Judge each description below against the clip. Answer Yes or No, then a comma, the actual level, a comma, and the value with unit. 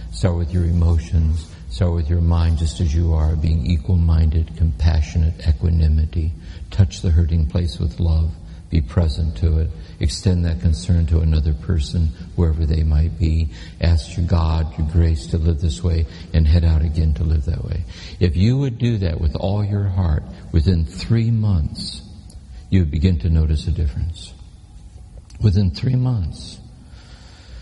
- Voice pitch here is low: Yes, very low, 85 Hz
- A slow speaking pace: No, average, 165 wpm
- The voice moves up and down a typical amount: No, narrow, 1.9 semitones